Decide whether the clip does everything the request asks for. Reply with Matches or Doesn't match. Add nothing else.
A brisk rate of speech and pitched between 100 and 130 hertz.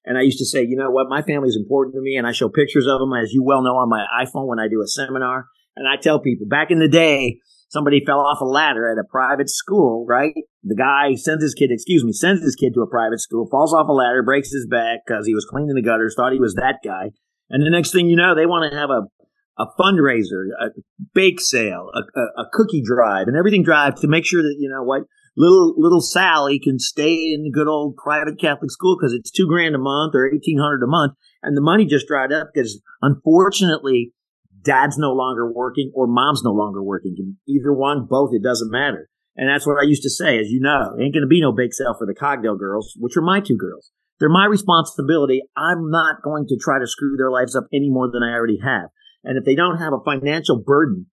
Doesn't match